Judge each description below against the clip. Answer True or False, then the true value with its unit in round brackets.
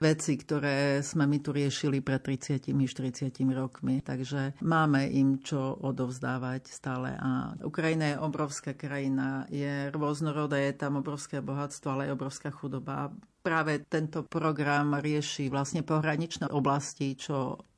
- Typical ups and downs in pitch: False (1.8 semitones)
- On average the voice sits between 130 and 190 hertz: True (140 Hz)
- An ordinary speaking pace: True (130 wpm)